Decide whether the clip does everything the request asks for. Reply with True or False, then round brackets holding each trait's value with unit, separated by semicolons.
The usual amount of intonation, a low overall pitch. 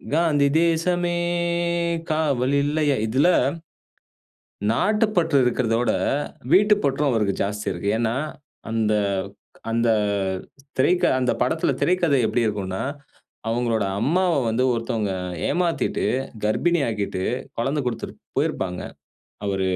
False (6.9 semitones; 130 Hz)